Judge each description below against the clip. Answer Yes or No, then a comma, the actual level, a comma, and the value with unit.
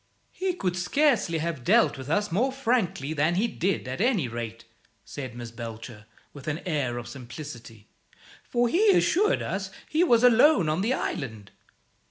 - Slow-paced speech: No, average, 165 wpm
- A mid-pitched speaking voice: Yes, medium, 170 Hz